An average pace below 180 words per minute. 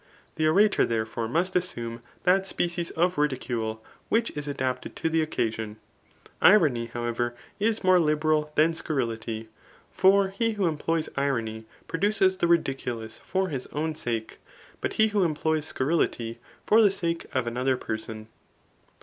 Yes: average, 140 wpm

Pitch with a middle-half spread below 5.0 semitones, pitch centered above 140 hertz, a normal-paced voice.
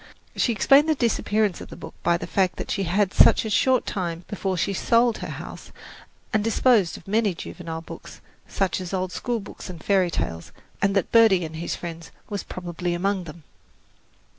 Yes: average, 3.7 semitones; high, 190 Hz; average, 180 wpm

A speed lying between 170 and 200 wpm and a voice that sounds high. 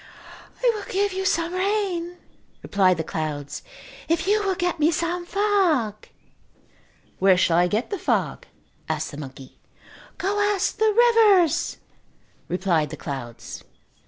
No: slow, 135 wpm; very high, 340 Hz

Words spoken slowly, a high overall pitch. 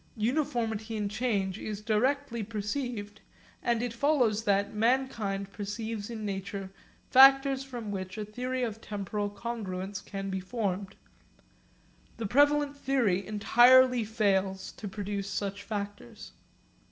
Yes: slow, 120 wpm; high, 215 Hz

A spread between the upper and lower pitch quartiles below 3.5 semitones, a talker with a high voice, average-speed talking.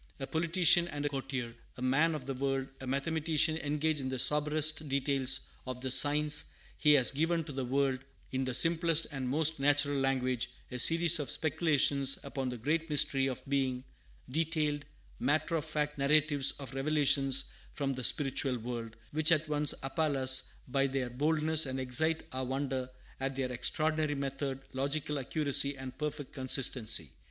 No: narrow, 2.6 semitones; medium, 140 Hz; average, 165 wpm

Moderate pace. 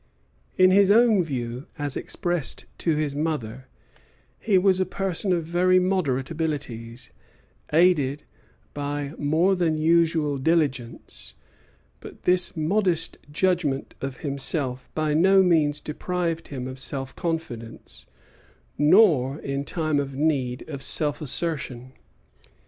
No: slow, 120 wpm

